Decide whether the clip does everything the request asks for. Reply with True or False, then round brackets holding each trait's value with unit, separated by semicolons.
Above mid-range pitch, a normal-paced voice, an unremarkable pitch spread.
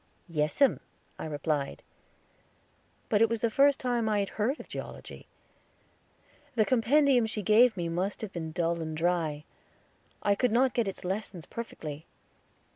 False (205 Hz; 160 wpm; 5.9 semitones)